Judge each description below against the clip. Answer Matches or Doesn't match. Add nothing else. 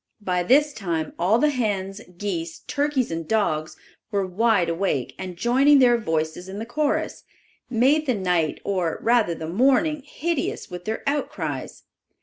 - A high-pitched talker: Matches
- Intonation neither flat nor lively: Doesn't match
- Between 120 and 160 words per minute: Matches